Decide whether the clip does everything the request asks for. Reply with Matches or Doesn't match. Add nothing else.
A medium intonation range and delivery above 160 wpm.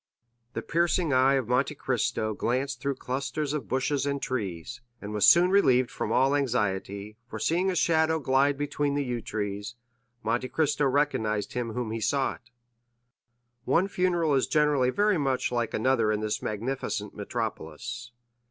Doesn't match